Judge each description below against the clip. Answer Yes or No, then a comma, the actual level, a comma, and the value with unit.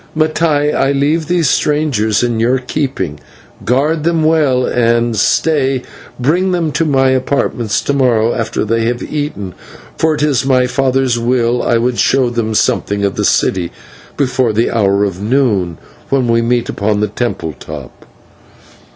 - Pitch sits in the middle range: No, low, 125 Hz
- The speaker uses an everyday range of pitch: Yes, average, 4.3 semitones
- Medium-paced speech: Yes, average, 160 wpm